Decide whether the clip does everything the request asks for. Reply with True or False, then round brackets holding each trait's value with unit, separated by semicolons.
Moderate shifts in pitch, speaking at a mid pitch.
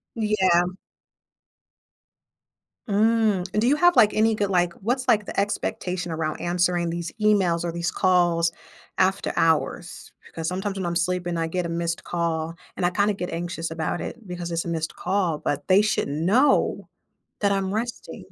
True (3.3 semitones; 180 Hz)